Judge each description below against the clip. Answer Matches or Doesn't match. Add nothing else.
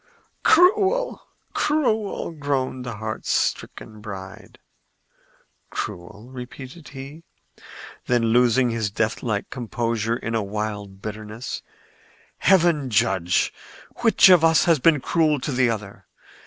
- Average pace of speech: Doesn't match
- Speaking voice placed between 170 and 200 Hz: Doesn't match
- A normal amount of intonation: Doesn't match